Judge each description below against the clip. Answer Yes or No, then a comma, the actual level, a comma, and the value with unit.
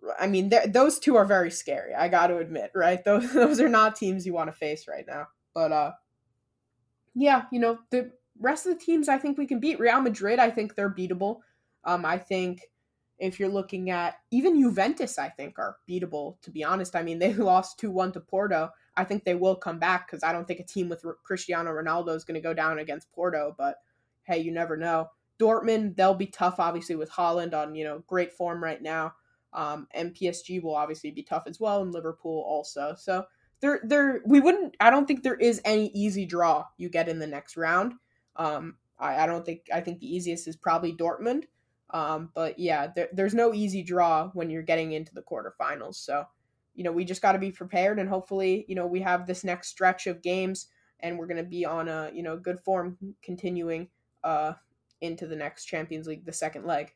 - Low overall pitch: No, medium, 180 Hz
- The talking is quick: Yes, fast, 220 wpm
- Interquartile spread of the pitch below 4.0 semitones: Yes, average, 3.6 semitones